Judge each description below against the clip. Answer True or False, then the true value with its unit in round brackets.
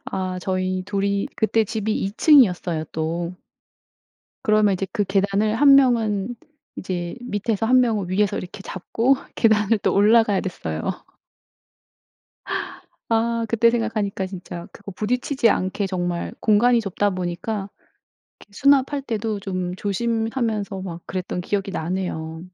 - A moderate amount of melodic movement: True (3.4 semitones)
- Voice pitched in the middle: False (205 Hz)